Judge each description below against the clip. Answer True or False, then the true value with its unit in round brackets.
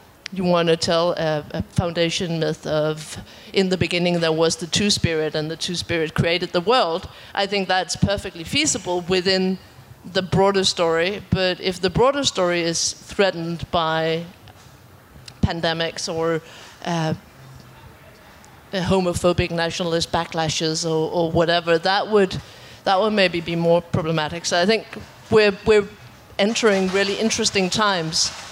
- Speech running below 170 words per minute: True (145 wpm)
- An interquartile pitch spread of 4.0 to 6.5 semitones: False (2.7 semitones)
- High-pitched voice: False (175 Hz)